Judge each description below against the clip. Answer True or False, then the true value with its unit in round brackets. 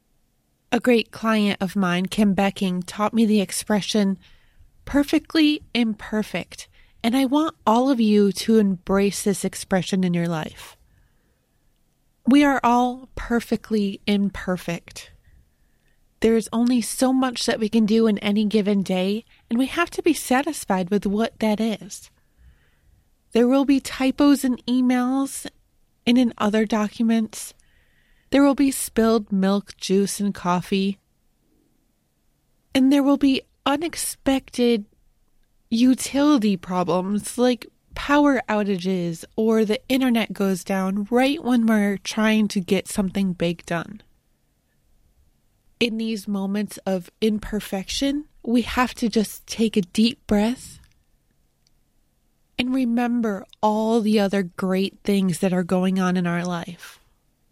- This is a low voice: False (220 Hz)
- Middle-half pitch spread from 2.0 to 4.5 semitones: True (3.9 semitones)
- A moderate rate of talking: False (130 wpm)